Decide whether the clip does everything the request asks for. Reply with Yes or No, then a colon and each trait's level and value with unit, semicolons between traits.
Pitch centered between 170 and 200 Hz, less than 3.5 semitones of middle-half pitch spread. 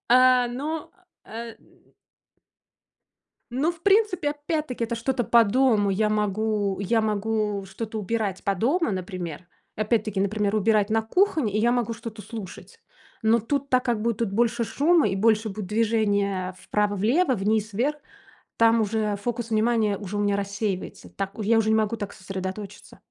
No: high, 220 Hz; average, 2.8 semitones